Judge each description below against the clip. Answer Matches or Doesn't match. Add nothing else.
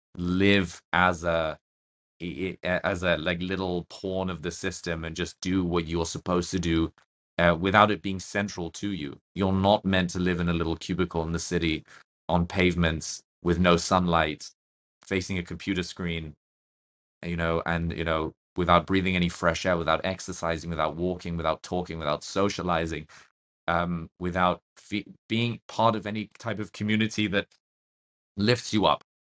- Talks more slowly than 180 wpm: Matches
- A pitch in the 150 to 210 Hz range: Doesn't match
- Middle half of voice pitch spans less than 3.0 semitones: Matches